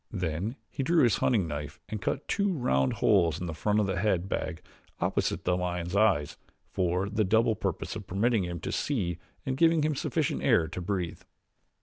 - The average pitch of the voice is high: No, very low, 95 Hz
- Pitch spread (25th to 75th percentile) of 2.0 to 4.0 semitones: No, average, 4.6 semitones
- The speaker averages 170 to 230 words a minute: Yes, average, 195 wpm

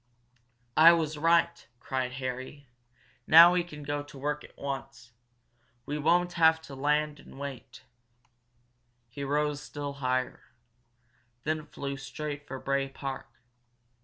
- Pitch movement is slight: Yes, narrow, 2.2 semitones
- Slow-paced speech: Yes, slow, 130 wpm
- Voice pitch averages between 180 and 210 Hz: No, medium, 145 Hz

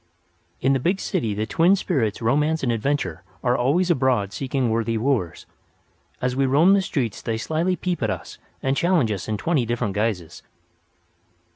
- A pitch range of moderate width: No, wide, 5.8 semitones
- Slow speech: No, average, 170 wpm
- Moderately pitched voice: No, low, 130 Hz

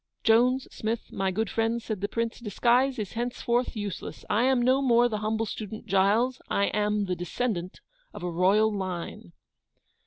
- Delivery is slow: No, average, 165 wpm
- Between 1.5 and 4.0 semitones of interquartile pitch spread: Yes, average, 3.3 semitones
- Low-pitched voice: No, high, 220 Hz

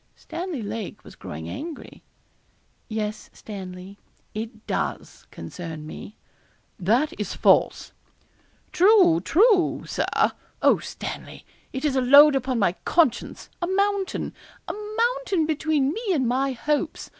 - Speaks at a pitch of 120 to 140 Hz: No, very high, 275 Hz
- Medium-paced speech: No, slow, 120 wpm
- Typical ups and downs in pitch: No, wide, 8.0 semitones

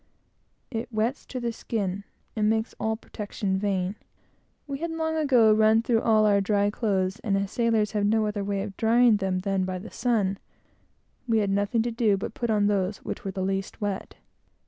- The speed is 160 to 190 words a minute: No, average, 200 wpm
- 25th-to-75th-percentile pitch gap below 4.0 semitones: Yes, narrow, 2.5 semitones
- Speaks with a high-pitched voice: Yes, high, 210 Hz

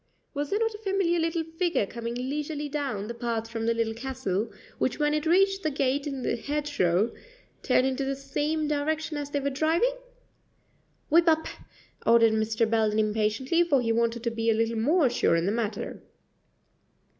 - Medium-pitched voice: No, very high, 270 Hz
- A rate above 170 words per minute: Yes, average, 180 wpm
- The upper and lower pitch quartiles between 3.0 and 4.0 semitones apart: No, average, 5.3 semitones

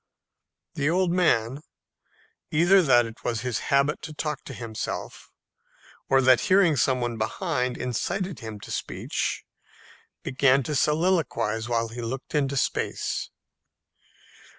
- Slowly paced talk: Yes, slow, 130 wpm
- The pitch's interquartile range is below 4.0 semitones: No, average, 4.6 semitones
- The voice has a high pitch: No, low, 135 Hz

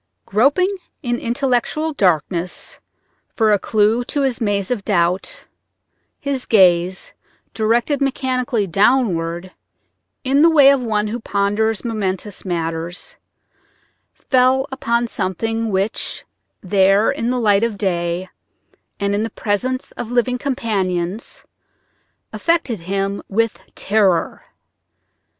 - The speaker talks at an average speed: No, slow, 110 wpm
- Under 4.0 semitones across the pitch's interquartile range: No, average, 4.6 semitones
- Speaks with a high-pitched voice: Yes, high, 220 Hz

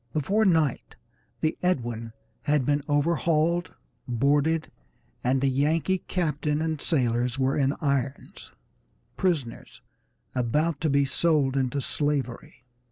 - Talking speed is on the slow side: Yes, slow, 110 wpm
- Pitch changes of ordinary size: Yes, average, 3.3 semitones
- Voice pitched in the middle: Yes, medium, 145 Hz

